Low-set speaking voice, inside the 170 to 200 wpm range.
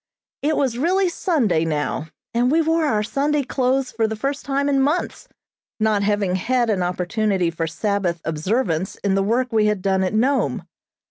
No: high, 220 Hz; average, 180 wpm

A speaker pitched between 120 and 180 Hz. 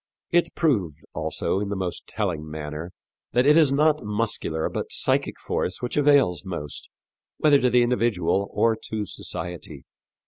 No: low, 105 Hz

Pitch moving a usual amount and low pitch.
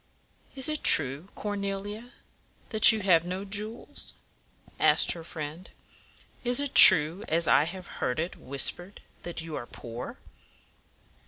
No: average, 4.7 semitones; medium, 185 Hz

